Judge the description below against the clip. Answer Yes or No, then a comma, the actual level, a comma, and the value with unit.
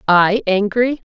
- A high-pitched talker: Yes, high, 210 Hz